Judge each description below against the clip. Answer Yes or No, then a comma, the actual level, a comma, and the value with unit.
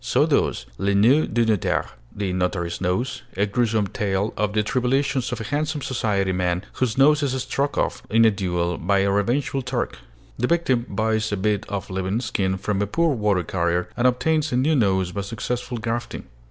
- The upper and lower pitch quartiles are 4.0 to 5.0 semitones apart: Yes, average, 4.6 semitones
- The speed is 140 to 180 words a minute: No, average, 195 wpm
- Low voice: Yes, low, 110 Hz